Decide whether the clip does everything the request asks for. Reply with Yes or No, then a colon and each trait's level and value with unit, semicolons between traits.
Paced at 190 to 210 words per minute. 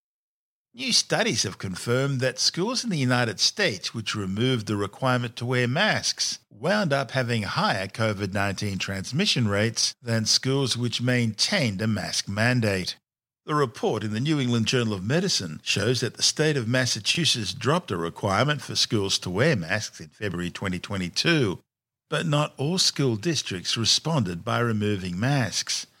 No: average, 150 wpm